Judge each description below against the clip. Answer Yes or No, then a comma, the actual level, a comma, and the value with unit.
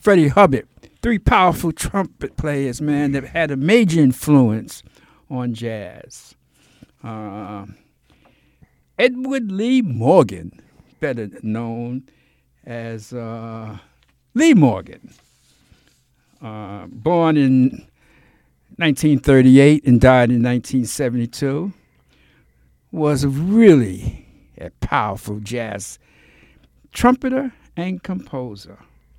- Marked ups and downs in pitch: Yes, wide, 6.7 semitones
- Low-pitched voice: Yes, low, 130 Hz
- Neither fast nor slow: No, slow, 80 wpm